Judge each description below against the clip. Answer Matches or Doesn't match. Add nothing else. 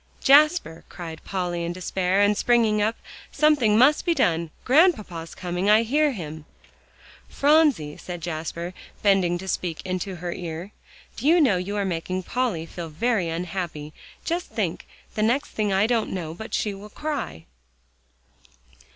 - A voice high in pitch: Matches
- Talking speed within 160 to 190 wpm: Doesn't match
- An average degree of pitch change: Doesn't match